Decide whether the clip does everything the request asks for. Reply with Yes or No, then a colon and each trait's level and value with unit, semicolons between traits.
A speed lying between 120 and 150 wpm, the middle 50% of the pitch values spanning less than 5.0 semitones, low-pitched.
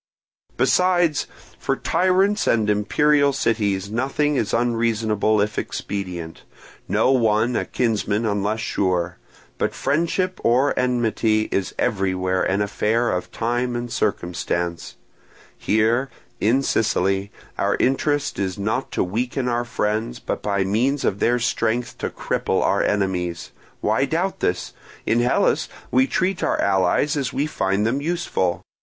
Yes: slow, 135 wpm; average, 4.5 semitones; low, 115 Hz